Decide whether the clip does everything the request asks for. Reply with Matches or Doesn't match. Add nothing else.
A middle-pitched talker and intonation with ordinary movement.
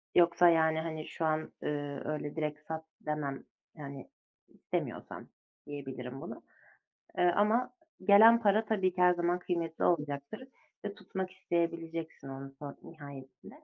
Matches